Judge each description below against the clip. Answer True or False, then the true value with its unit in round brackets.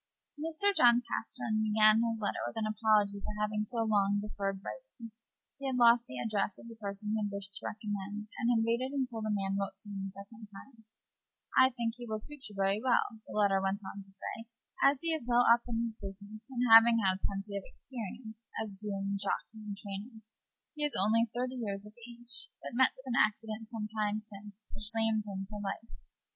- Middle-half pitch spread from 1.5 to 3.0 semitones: True (2.6 semitones)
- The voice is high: True (215 Hz)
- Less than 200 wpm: False (205 wpm)